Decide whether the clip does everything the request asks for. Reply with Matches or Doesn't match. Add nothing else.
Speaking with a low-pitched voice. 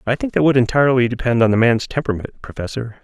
Matches